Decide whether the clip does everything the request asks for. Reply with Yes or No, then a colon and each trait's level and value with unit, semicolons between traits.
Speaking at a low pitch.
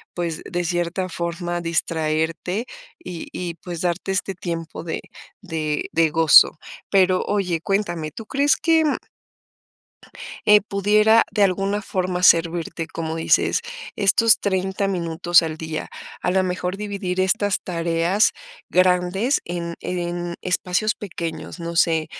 No: medium, 180 Hz